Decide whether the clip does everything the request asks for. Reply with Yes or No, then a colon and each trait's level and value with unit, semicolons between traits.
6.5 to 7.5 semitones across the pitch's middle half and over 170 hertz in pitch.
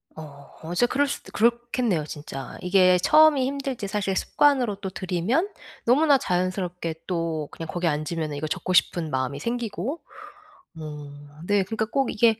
Yes: wide, 7.1 semitones; medium, 185 Hz